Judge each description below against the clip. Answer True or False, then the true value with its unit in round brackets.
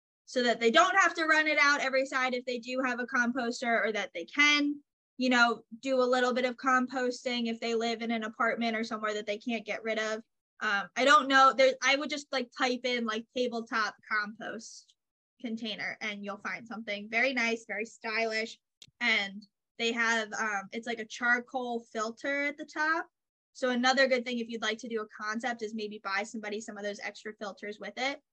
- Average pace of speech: False (210 wpm)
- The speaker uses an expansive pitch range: False (2.9 semitones)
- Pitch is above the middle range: True (235 Hz)